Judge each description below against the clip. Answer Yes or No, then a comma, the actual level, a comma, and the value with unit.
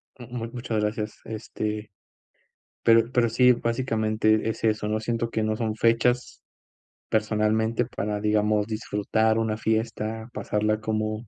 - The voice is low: Yes, low, 110 Hz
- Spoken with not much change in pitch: Yes, narrow, 1.2 semitones